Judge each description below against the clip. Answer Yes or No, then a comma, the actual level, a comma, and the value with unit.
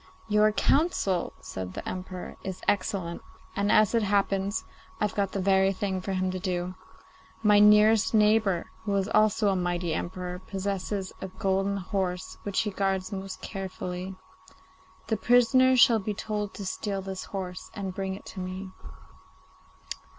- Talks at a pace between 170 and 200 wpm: No, average, 155 wpm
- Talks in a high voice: Yes, high, 195 Hz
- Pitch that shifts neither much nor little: No, narrow, 2.0 semitones